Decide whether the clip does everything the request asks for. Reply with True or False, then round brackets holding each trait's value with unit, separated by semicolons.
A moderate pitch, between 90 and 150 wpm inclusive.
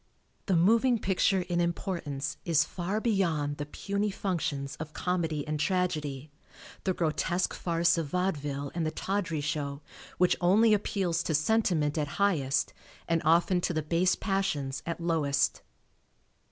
True (170 Hz; 140 wpm)